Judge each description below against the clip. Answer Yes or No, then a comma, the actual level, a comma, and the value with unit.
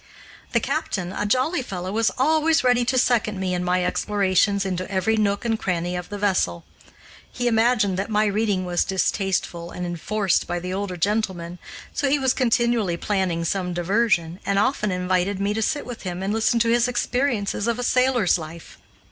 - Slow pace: No, average, 185 wpm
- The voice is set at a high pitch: Yes, high, 200 Hz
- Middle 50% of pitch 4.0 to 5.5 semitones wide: Yes, average, 4.3 semitones